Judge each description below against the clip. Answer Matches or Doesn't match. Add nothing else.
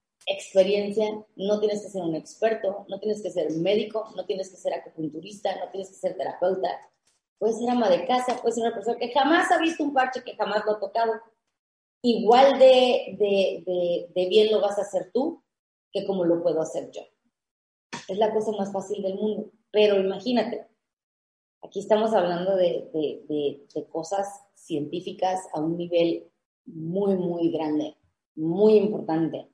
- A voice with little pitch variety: Doesn't match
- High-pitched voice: Matches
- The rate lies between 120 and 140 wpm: Doesn't match